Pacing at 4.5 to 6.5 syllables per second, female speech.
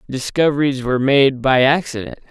No: 5.4 syllables/s; male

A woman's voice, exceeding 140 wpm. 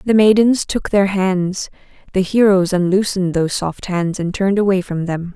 Yes: female; average, 180 wpm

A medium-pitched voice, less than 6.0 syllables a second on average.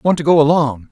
Yes: medium, 150 Hz; 5.8 syllables/s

